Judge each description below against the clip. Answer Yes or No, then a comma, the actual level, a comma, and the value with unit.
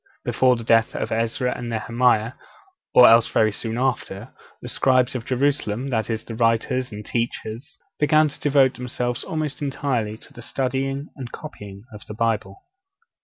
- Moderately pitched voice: No, low, 120 Hz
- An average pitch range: Yes, average, 3.0 semitones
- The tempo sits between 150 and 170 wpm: Yes, average, 165 wpm